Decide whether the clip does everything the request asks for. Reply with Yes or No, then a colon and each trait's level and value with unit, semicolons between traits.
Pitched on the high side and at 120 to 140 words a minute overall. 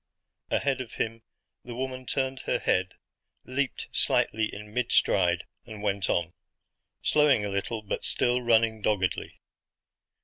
No: low, 110 Hz; slow, 135 wpm